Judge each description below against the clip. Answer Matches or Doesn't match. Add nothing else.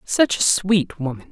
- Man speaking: Matches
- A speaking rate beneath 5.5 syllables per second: Matches